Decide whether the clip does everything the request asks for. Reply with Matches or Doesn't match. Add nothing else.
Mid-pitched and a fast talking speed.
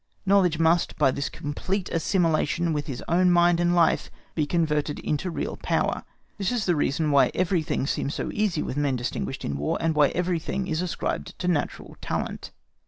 Doesn't match